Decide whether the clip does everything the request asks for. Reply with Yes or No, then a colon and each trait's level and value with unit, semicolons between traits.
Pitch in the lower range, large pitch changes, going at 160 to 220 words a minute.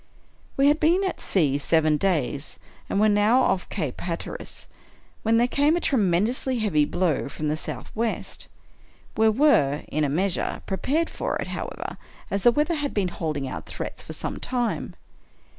No: high, 200 Hz; wide, 8.6 semitones; average, 165 wpm